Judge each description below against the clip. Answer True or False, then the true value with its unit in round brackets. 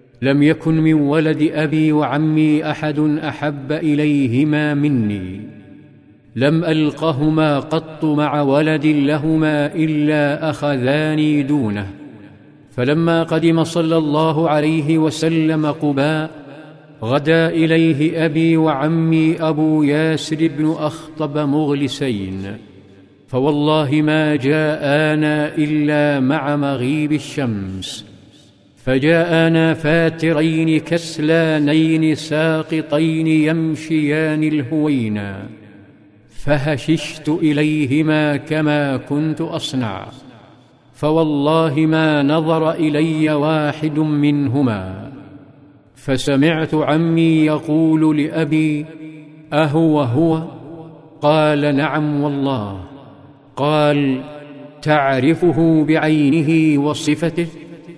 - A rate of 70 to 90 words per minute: True (75 wpm)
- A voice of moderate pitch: True (150 Hz)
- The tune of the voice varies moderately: False (1.7 semitones)